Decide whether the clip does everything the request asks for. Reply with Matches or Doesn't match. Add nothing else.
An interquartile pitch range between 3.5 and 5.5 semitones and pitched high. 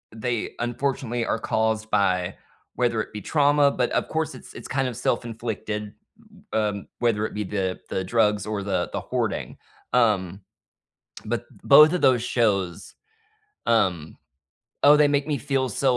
Doesn't match